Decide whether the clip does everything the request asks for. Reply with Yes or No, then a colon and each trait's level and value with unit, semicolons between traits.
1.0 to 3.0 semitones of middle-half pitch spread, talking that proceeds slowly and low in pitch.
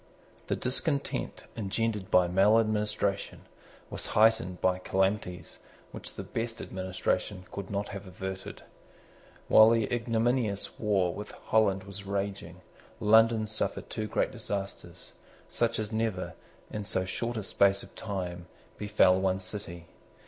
Yes: average, 2.7 semitones; slow, 125 wpm; low, 100 Hz